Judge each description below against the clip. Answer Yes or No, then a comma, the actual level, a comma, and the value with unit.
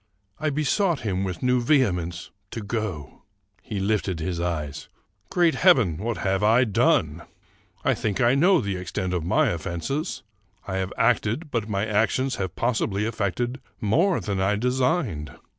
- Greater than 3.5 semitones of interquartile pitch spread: Yes, average, 5.2 semitones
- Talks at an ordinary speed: Yes, average, 160 wpm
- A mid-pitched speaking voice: No, low, 105 Hz